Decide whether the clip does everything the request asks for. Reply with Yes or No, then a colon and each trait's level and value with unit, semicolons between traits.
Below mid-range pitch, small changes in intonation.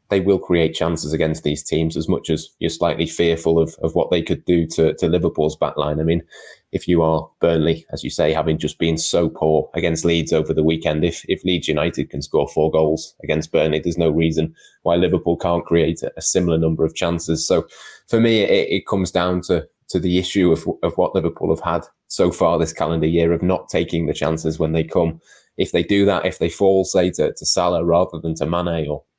Yes: very low, 80 Hz; narrow, 1.4 semitones